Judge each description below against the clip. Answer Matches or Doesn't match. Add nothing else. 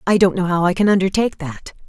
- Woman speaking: Matches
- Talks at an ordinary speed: Doesn't match